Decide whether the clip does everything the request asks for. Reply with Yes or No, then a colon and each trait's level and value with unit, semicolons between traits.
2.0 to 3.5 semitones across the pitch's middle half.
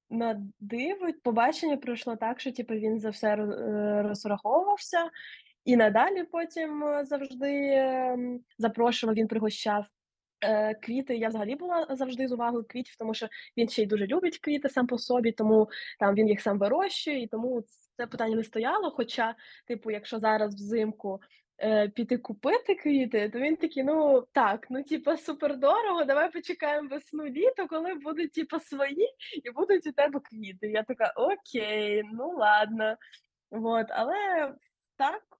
No: wide, 5.5 semitones